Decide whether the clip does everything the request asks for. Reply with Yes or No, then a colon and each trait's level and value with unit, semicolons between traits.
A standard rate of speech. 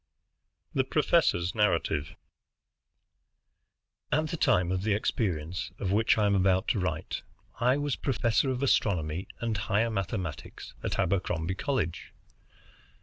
No: slow, 125 wpm